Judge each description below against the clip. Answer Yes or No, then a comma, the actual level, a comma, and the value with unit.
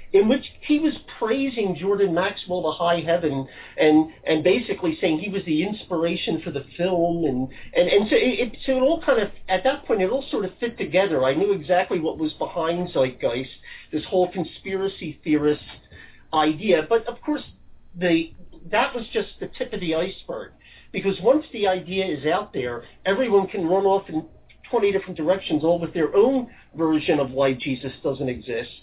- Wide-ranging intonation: No, average, 4.2 semitones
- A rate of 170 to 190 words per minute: Yes, average, 185 wpm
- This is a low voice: No, medium, 180 Hz